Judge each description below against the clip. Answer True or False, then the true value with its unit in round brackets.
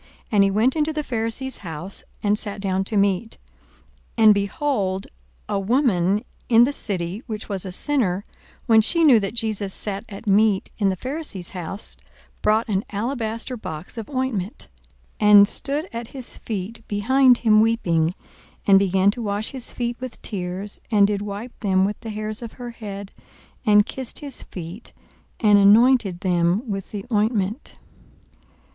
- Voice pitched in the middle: False (210 Hz)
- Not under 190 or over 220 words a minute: False (165 wpm)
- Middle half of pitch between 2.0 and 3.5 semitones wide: True (3.2 semitones)